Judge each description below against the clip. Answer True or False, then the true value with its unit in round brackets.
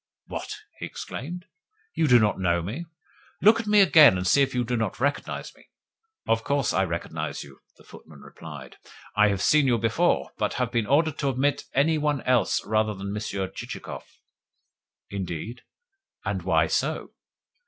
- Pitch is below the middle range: True (115 Hz)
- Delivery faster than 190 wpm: False (170 wpm)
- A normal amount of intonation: False (6.5 semitones)